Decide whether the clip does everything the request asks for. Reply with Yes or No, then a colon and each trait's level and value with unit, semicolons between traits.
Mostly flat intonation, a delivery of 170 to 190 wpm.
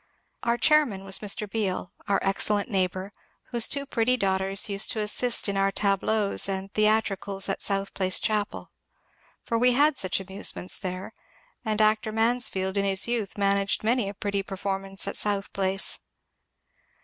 No: narrow, 2.1 semitones; average, 160 wpm